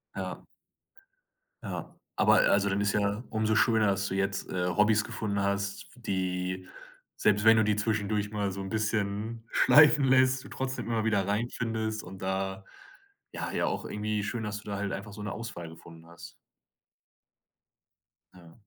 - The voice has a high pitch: No, low, 105 Hz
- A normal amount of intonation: No, narrow, 2.2 semitones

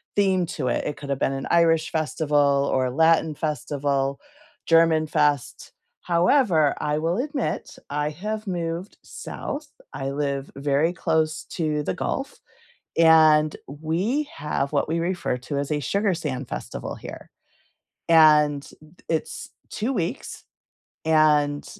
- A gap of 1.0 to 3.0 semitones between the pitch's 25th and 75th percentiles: Yes, narrow, 2.6 semitones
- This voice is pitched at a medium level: Yes, medium, 155 Hz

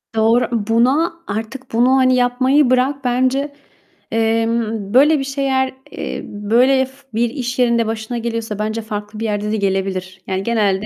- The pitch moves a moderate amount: Yes, average, 3.2 semitones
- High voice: Yes, high, 235 Hz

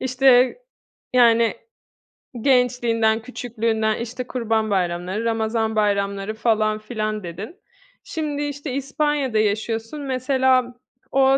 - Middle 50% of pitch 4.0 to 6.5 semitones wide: No, average, 3.2 semitones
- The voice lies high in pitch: Yes, high, 230 Hz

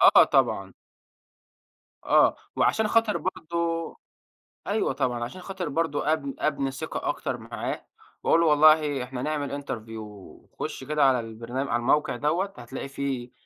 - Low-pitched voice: No, medium, 145 Hz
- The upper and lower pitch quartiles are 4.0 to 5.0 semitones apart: Yes, average, 4.3 semitones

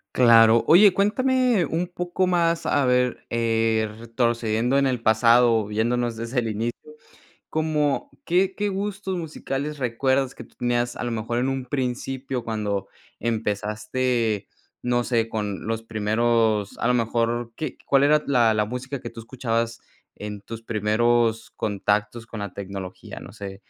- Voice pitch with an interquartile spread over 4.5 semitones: No, average, 3.3 semitones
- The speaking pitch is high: No, low, 120 Hz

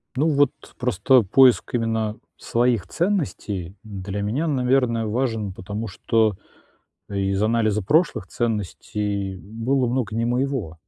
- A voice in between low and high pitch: No, low, 115 Hz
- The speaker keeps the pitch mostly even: No, average, 3.8 semitones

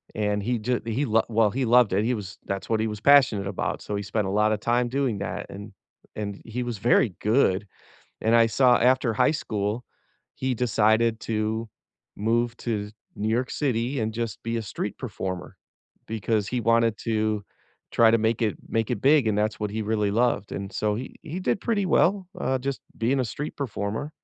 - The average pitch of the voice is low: Yes, low, 115 Hz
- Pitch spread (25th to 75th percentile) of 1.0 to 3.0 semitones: Yes, average, 2.7 semitones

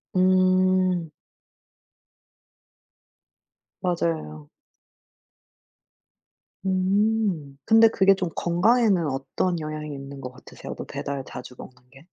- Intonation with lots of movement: No, average, 4.9 semitones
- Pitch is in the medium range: Yes, medium, 175 Hz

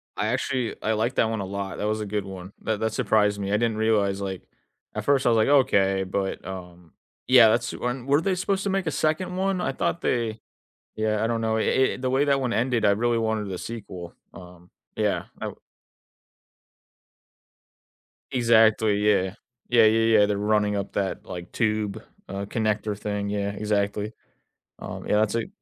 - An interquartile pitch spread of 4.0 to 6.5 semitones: No, average, 2.8 semitones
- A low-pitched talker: Yes, low, 110 Hz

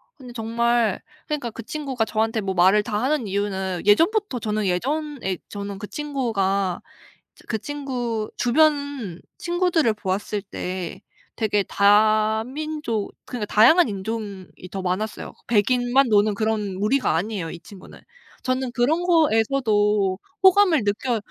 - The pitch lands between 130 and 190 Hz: No, high, 220 Hz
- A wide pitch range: No, average, 4.7 semitones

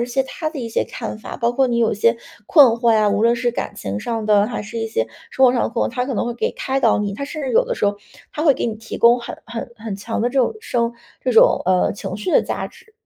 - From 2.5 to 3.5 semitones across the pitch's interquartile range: Yes, average, 2.9 semitones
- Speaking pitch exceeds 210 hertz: Yes, high, 235 Hz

